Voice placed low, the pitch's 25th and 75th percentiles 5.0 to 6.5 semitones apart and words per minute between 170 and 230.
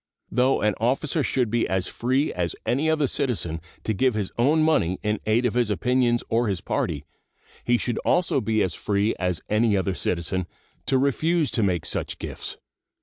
Yes: low, 115 Hz; wide, 5.4 semitones; average, 185 wpm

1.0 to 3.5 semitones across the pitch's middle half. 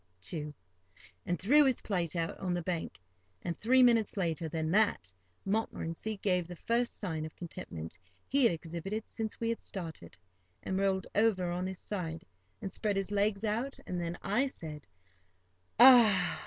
No: average, 4.7 semitones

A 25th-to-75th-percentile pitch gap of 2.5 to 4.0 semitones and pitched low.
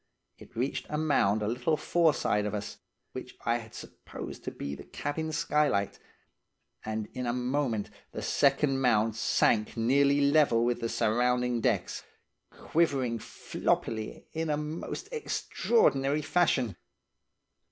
No: average, 4.8 semitones; low, 125 Hz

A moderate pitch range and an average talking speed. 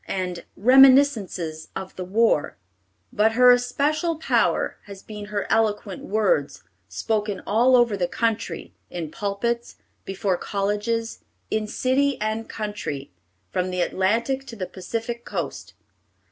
No: average, 3.8 semitones; slow, 130 wpm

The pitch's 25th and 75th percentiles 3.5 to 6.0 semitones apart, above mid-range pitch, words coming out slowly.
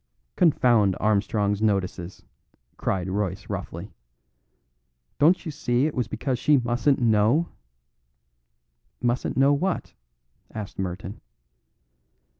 No: wide, 5.5 semitones; low, 115 Hz; slow, 95 wpm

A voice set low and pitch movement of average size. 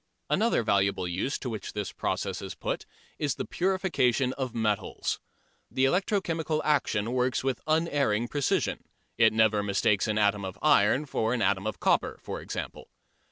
No: low, 120 Hz; wide, 5.9 semitones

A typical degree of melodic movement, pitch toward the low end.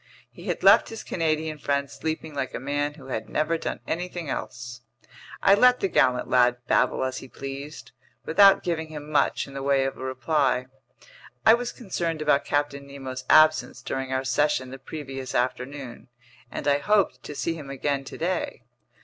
No: average, 3.2 semitones; medium, 145 Hz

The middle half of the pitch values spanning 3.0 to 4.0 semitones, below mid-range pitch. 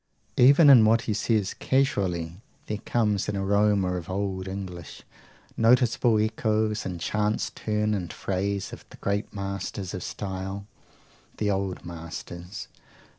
No: narrow, 2.4 semitones; low, 100 Hz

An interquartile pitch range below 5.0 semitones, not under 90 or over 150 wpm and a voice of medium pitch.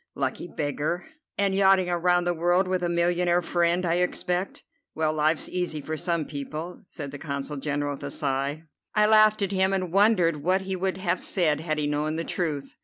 No: average, 3.3 semitones; average, 195 wpm; medium, 170 Hz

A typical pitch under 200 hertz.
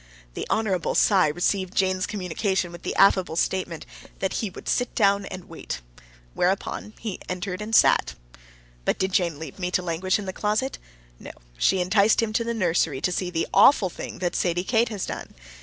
Yes: medium, 185 Hz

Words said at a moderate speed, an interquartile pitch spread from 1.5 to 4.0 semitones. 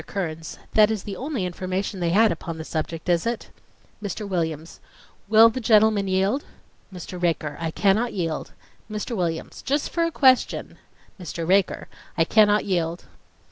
No: average, 155 wpm; average, 4.4 semitones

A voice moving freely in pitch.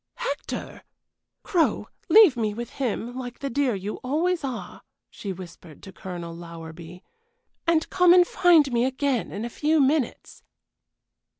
Yes: wide, 8.4 semitones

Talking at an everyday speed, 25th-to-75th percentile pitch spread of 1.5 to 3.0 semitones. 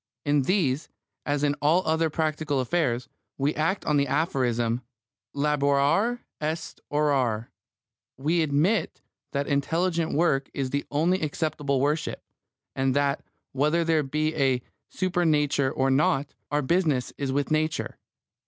No: slow, 130 wpm; average, 2.7 semitones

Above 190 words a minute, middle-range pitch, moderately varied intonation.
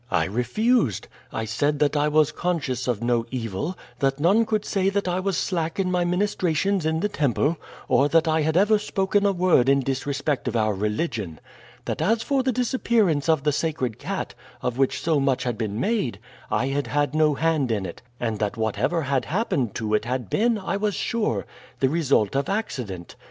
No: average, 200 wpm; medium, 150 Hz; wide, 7.2 semitones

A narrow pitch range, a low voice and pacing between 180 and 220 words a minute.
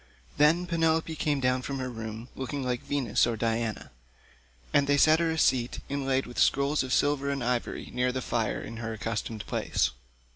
No: average, 3.4 semitones; low, 130 Hz; average, 185 wpm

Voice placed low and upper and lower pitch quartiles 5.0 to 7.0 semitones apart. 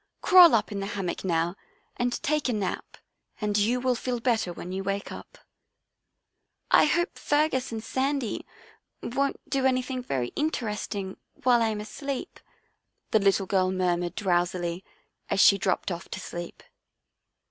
No: high, 210 Hz; wide, 5.4 semitones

